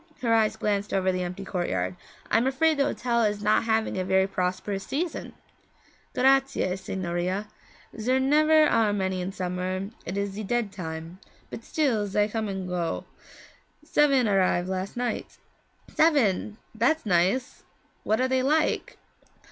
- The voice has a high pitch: Yes, high, 205 Hz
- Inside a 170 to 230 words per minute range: No, average, 155 wpm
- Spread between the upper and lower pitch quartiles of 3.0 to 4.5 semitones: No, average, 5.3 semitones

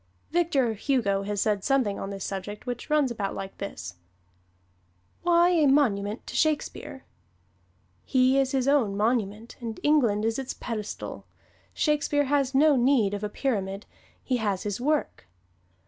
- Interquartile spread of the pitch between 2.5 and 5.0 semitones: No, wide, 5.4 semitones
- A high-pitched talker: Yes, high, 240 Hz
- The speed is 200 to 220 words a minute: No, average, 145 wpm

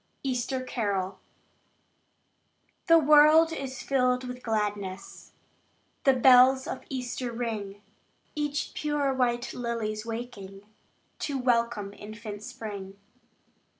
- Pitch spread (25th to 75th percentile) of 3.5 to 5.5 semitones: Yes, average, 4.0 semitones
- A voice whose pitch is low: No, high, 240 Hz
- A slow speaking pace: Yes, slow, 95 wpm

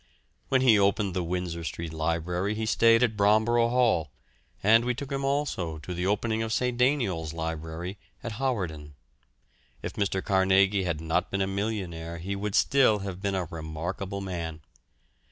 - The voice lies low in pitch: Yes, very low, 95 Hz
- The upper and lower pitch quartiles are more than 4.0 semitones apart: Yes, average, 4.9 semitones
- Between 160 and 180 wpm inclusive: Yes, average, 165 wpm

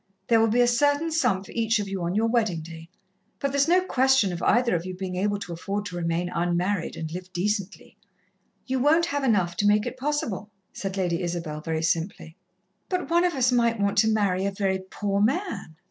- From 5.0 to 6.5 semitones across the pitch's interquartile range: Yes, wide, 5.6 semitones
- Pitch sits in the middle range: No, high, 205 Hz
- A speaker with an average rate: No, fast, 215 wpm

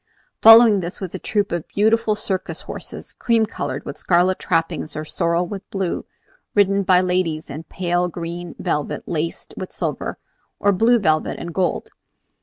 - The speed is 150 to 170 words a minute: Yes, average, 160 wpm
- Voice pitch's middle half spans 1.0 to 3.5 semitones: Yes, average, 3.2 semitones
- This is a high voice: No, medium, 180 Hz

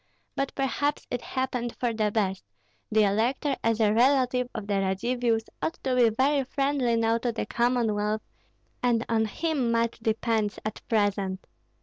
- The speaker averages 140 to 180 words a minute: Yes, average, 155 wpm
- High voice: Yes, high, 230 Hz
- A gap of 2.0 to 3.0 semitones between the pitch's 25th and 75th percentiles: Yes, average, 2.7 semitones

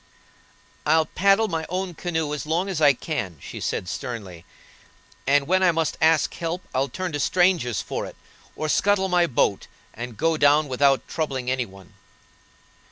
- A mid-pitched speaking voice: Yes, medium, 155 Hz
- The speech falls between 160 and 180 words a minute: Yes, average, 165 wpm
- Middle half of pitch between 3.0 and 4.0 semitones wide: No, average, 5.2 semitones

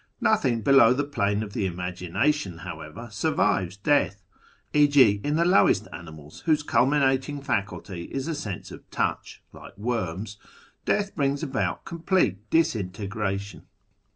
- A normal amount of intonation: No, wide, 6.9 semitones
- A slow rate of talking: Yes, slow, 130 wpm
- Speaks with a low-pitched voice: Yes, low, 110 Hz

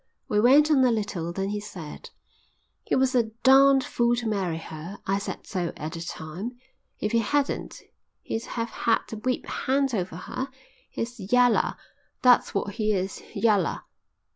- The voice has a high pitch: Yes, high, 215 Hz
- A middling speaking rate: Yes, average, 165 wpm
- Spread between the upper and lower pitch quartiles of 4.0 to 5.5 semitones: Yes, average, 4.5 semitones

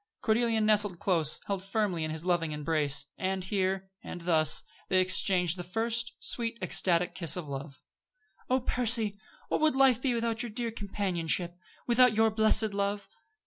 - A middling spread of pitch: Yes, average, 4.4 semitones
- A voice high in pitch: Yes, high, 195 Hz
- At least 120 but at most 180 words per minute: Yes, average, 160 wpm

